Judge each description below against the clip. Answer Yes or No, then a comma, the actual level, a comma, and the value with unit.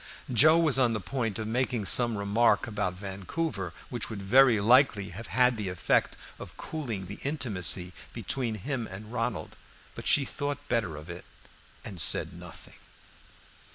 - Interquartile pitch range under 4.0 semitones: No, average, 4.7 semitones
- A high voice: No, low, 115 Hz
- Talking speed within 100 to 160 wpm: Yes, average, 155 wpm